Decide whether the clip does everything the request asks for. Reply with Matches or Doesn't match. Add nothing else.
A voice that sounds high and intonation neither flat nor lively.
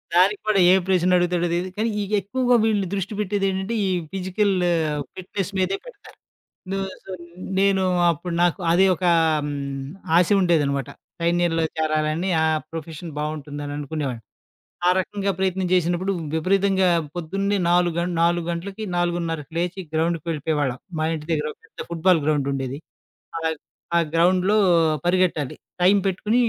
Doesn't match